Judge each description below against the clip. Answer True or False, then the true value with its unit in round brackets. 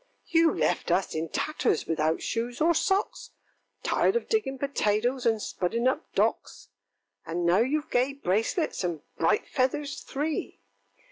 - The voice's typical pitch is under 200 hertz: False (250 Hz)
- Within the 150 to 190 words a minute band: False (140 wpm)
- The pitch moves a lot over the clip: True (7.9 semitones)